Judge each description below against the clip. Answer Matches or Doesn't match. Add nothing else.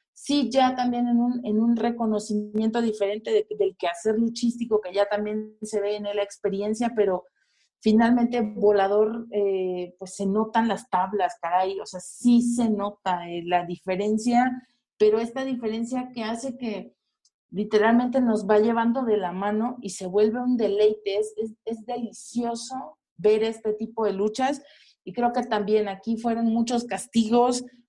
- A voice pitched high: Matches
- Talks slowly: Doesn't match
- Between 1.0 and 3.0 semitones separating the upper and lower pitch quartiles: Matches